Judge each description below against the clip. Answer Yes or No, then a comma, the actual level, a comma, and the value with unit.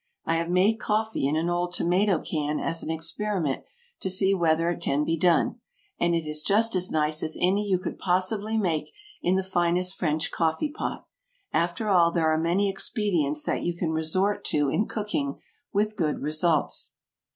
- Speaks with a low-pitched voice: No, medium, 175 Hz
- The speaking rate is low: No, average, 185 wpm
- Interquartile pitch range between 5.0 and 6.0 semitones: No, average, 3.5 semitones